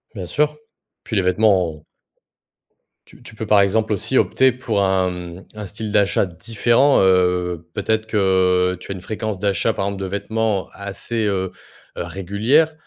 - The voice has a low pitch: Yes, low, 100 Hz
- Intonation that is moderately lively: Yes, average, 3.1 semitones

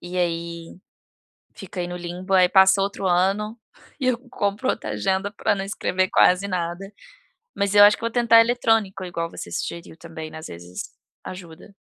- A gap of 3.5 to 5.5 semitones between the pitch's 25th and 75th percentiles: No, average, 2.7 semitones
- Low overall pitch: No, high, 190 Hz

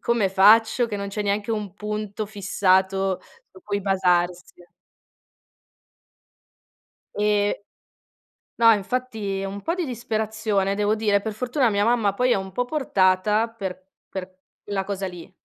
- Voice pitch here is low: No, high, 205 Hz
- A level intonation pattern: Yes, narrow, 2.3 semitones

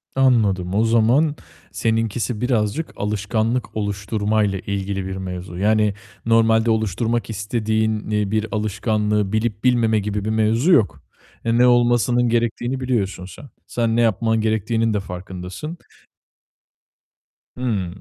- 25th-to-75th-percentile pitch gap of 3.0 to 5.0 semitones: No, narrow, 2.5 semitones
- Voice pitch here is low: Yes, low, 110 Hz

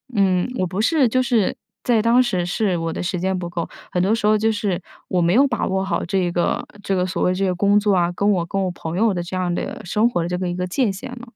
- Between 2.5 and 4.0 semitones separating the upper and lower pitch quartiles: Yes, average, 3.3 semitones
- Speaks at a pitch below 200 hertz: Yes, high, 190 Hz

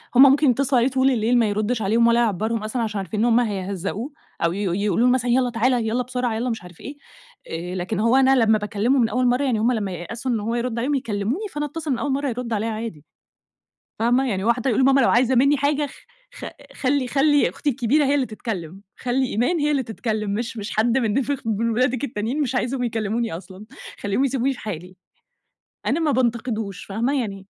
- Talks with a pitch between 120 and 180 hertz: No, high, 235 Hz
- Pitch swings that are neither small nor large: Yes, average, 3.5 semitones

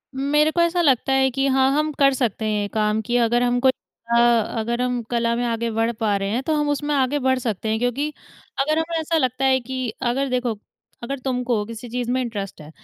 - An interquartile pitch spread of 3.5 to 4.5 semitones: No, average, 2.7 semitones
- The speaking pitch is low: No, very high, 250 Hz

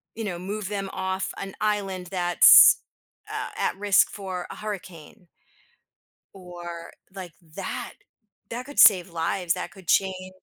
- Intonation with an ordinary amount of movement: No, narrow, 2.1 semitones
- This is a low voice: No, high, 190 Hz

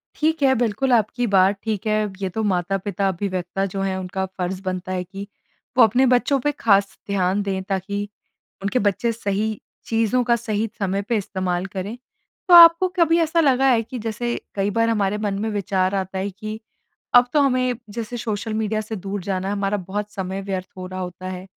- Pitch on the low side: No, high, 205 Hz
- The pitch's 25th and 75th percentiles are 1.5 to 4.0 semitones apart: Yes, average, 3.3 semitones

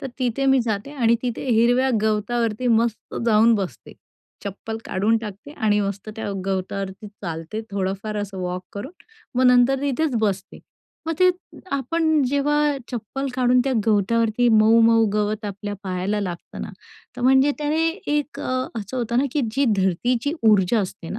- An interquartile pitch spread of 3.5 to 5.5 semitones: Yes, average, 4.2 semitones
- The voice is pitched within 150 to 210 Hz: No, high, 225 Hz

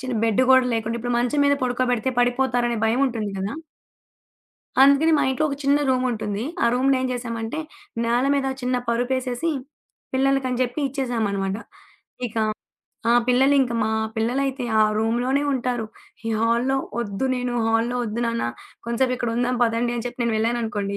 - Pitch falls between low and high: No, high, 245 Hz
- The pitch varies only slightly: Yes, narrow, 2.2 semitones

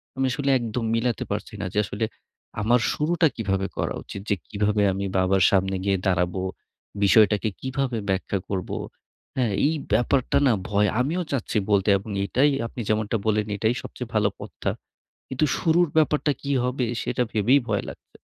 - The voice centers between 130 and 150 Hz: No, low, 110 Hz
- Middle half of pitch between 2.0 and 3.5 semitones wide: No, average, 4.8 semitones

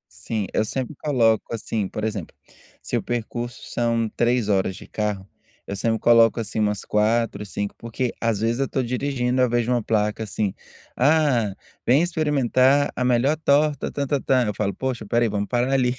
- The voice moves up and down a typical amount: Yes, average, 3.3 semitones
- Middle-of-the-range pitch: No, low, 120 Hz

